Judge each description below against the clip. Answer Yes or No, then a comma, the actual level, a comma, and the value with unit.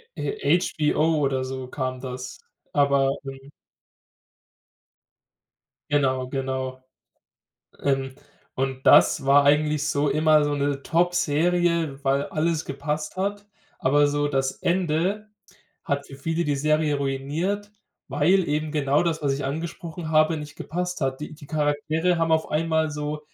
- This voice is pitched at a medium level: Yes, medium, 150 Hz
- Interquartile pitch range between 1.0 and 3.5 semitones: Yes, average, 2.9 semitones